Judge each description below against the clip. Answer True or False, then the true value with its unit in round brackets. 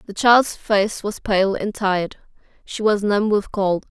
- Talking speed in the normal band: True (180 wpm)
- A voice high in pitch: True (205 Hz)